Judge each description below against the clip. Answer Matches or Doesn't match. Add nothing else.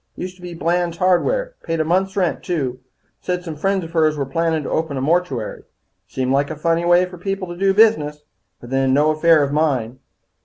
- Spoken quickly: Matches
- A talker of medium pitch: Matches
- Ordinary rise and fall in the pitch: Matches